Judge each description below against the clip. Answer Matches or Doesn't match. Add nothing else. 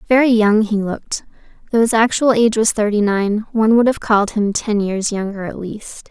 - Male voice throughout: Doesn't match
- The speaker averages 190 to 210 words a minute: Matches